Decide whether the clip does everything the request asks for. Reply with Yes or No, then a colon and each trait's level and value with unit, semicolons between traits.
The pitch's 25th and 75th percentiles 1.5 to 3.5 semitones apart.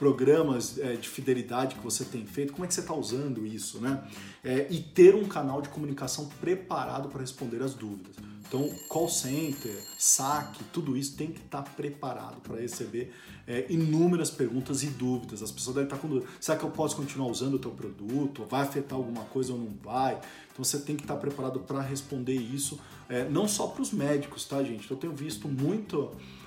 Yes: average, 2.7 semitones